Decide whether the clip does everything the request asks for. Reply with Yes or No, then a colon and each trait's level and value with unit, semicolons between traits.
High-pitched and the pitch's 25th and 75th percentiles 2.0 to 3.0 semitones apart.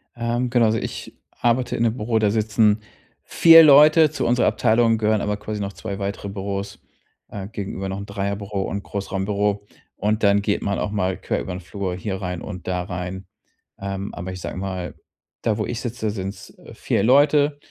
No: low, 105 Hz; narrow, 2.6 semitones